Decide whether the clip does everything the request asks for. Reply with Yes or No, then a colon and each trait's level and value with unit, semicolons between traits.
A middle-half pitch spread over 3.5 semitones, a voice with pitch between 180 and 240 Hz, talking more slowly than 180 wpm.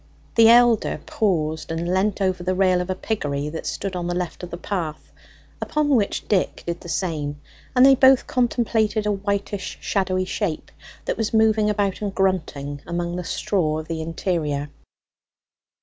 Yes: average, 4.2 semitones; medium, 185 Hz; average, 170 wpm